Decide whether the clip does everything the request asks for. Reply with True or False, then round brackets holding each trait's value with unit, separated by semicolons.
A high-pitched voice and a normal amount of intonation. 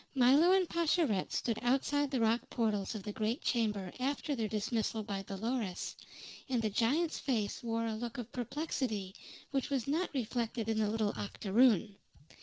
True (230 Hz; 3.8 semitones)